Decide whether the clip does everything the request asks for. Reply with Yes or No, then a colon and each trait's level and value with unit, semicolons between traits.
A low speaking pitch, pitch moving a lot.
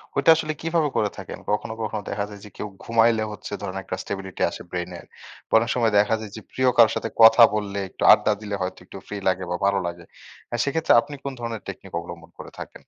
No: low, 105 Hz; average, 3.1 semitones